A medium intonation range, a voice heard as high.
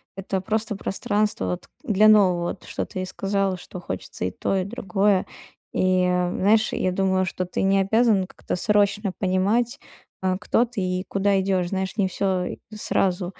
No: narrow, 1.9 semitones; high, 195 Hz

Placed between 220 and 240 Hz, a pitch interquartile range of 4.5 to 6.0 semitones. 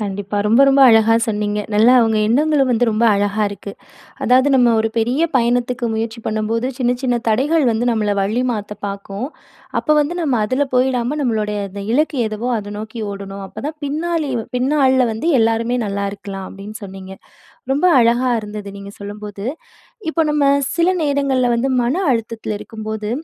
No: high, 230 Hz; average, 3.7 semitones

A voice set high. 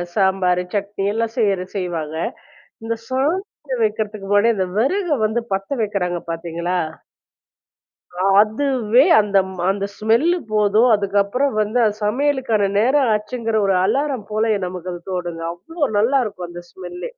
Yes: high, 210 Hz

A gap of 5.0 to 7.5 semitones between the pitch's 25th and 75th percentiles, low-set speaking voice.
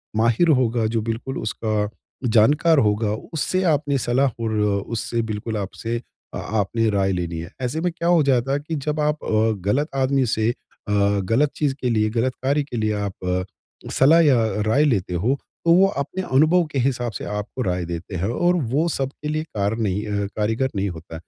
Yes: wide, 5.5 semitones; low, 115 Hz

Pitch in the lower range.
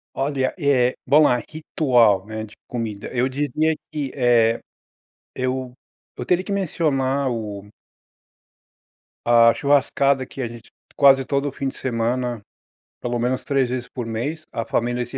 Yes: low, 130 Hz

